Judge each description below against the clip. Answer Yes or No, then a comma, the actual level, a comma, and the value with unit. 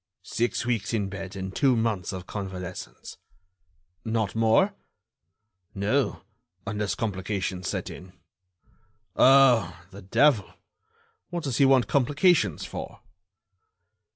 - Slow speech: Yes, slow, 105 wpm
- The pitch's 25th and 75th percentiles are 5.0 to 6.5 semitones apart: Yes, average, 5.3 semitones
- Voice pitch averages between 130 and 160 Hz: No, low, 110 Hz